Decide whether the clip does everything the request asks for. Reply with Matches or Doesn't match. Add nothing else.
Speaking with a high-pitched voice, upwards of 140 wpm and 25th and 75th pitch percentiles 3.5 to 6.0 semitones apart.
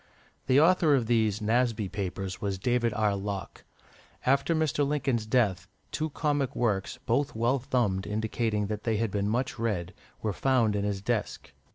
Doesn't match